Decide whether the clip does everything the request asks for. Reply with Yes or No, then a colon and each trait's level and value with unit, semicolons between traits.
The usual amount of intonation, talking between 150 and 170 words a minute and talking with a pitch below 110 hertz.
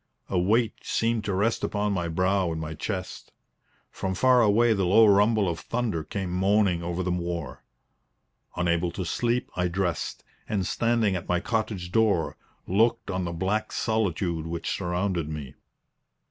Yes: average, 3.8 semitones; average, 160 wpm; very low, 95 Hz